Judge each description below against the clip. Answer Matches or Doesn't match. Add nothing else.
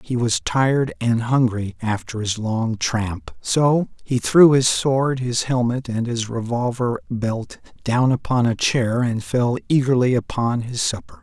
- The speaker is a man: Matches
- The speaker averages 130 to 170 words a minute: Matches